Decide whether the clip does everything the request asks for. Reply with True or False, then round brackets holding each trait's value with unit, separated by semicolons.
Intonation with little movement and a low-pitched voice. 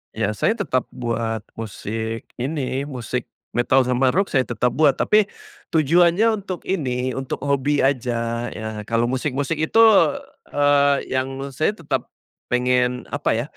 False (3.2 semitones; 130 Hz)